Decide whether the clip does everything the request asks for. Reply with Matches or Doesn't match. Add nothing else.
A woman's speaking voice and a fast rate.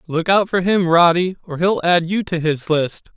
Doesn't match